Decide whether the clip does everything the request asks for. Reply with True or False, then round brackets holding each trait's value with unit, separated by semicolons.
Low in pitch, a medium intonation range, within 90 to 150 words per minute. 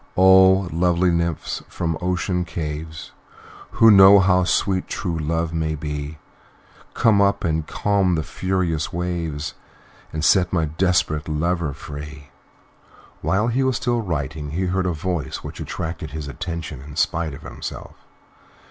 True (85 Hz; 3.3 semitones; 140 wpm)